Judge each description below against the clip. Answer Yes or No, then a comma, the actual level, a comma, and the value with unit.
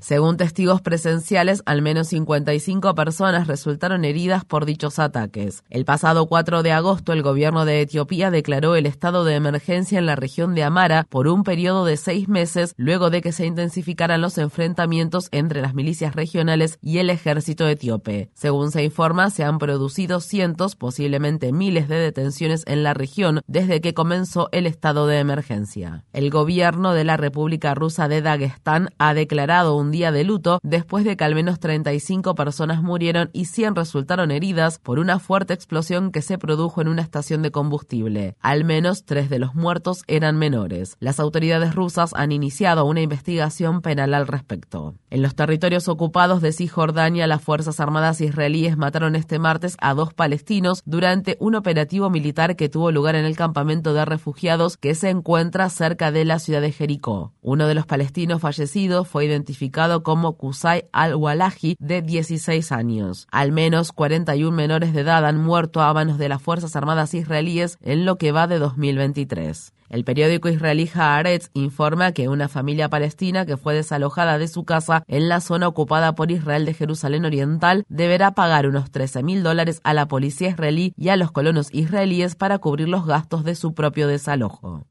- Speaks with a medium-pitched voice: Yes, medium, 160 Hz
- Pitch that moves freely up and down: No, average, 2.7 semitones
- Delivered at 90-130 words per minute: No, average, 175 wpm